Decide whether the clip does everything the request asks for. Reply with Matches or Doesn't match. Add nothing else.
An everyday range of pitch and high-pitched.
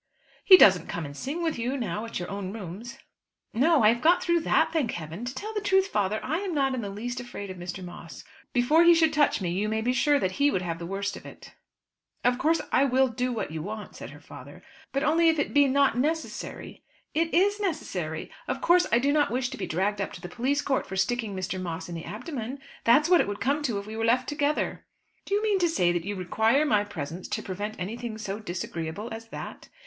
Doesn't match